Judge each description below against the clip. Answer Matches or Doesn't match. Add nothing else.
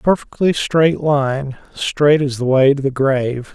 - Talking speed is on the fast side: Doesn't match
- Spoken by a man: Matches